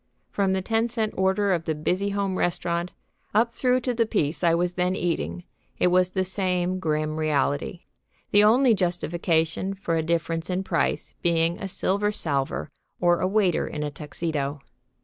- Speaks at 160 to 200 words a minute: Yes, average, 170 wpm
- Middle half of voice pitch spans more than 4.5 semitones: No, average, 3.3 semitones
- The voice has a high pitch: No, medium, 180 Hz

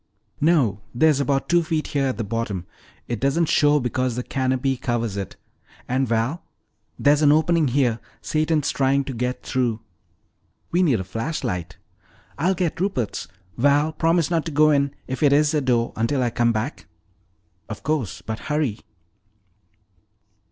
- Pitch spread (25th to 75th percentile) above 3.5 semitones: Yes, average, 4.4 semitones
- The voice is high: No, low, 135 Hz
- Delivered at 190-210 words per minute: No, average, 160 wpm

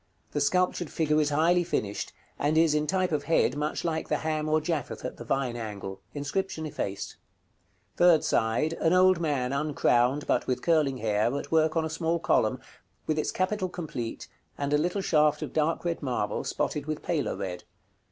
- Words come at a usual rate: Yes, average, 185 wpm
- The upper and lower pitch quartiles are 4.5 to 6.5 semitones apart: No, average, 3.3 semitones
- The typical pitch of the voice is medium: Yes, medium, 155 Hz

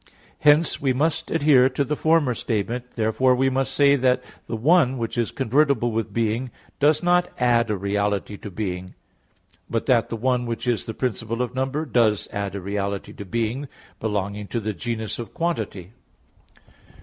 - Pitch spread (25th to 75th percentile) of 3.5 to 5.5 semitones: Yes, average, 3.8 semitones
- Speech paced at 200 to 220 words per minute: No, average, 175 wpm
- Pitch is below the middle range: Yes, low, 120 Hz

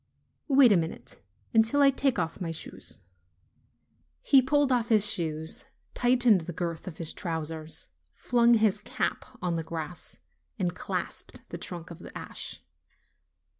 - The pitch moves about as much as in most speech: No, wide, 6.7 semitones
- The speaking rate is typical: Yes, average, 145 wpm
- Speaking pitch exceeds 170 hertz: Yes, medium, 185 Hz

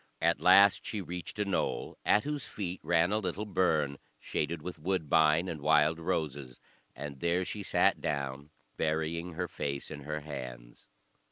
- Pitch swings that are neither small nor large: Yes, average, 3.8 semitones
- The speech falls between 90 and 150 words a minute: No, average, 160 wpm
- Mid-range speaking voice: No, very low, 80 Hz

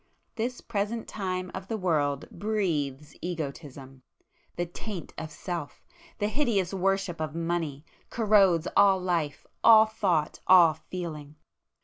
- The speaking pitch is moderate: Yes, medium, 180 Hz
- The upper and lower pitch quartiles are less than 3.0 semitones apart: No, average, 4.5 semitones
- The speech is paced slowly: Yes, slow, 115 wpm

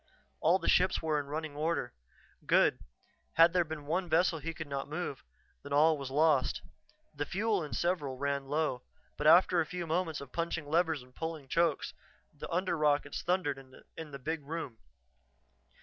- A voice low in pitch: No, medium, 155 Hz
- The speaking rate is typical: Yes, average, 175 wpm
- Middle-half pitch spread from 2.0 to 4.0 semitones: Yes, average, 2.9 semitones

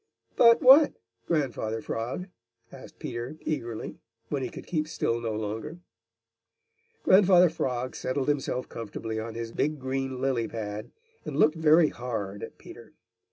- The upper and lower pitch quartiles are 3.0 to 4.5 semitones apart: No, average, 5.2 semitones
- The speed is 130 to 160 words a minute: Yes, average, 140 wpm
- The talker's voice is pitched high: No, low, 130 Hz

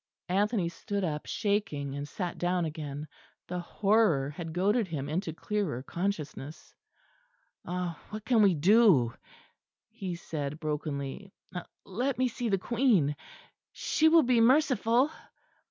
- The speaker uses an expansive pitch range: Yes, wide, 6.1 semitones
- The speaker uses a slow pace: Yes, slow, 125 wpm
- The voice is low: No, medium, 180 Hz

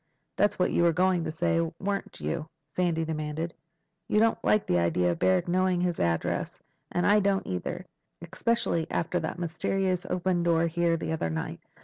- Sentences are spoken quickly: No, average, 175 wpm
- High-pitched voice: No, medium, 170 Hz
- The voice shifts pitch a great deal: No, average, 2.7 semitones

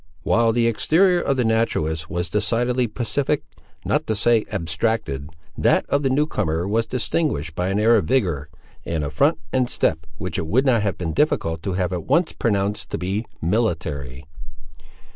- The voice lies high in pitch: No, low, 105 Hz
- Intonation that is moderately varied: No, wide, 6.8 semitones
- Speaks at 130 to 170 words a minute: No, average, 180 wpm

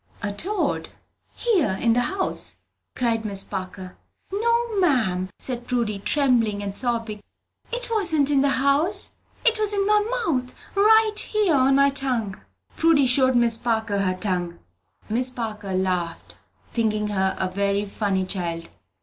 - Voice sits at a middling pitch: No, high, 240 Hz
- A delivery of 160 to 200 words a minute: No, average, 145 wpm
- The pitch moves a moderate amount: No, wide, 7.7 semitones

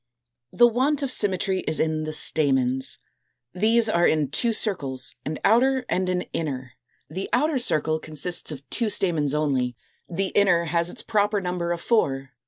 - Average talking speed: Yes, average, 165 wpm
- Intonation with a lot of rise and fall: Yes, wide, 5.9 semitones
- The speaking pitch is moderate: Yes, medium, 175 Hz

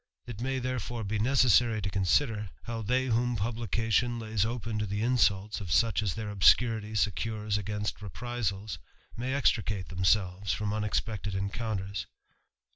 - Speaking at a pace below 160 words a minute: Yes, average, 140 wpm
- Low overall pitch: Yes, low, 110 Hz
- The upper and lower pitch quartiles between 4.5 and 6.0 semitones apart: No, average, 2.7 semitones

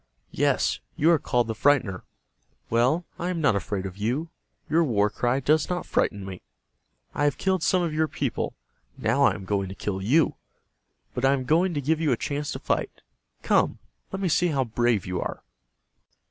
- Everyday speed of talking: Yes, average, 195 wpm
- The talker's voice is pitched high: No, low, 135 Hz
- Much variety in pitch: Yes, wide, 7.2 semitones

